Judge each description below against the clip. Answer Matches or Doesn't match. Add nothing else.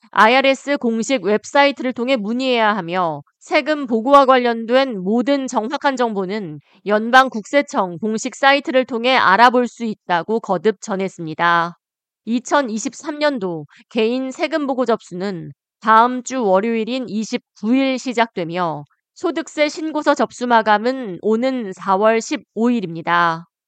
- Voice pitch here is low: Doesn't match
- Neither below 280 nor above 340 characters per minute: Doesn't match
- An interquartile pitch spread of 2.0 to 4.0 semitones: Doesn't match